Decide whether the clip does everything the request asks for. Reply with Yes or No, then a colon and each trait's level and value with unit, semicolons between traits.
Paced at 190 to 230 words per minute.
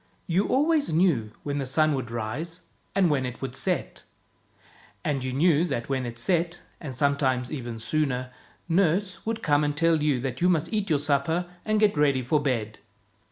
Yes: average, 195 wpm